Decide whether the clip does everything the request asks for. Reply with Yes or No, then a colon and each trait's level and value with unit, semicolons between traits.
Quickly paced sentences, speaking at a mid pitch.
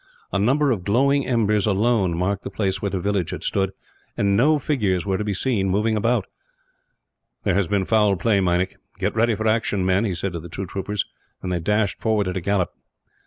No: fast, 215 wpm; low, 100 Hz